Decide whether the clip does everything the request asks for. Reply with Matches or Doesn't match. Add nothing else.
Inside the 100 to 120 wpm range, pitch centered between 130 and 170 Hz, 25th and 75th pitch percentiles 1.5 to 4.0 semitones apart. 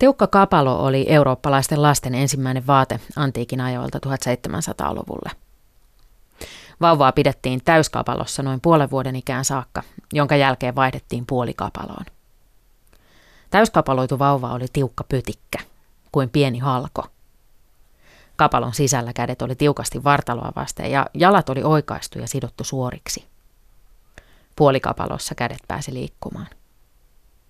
Matches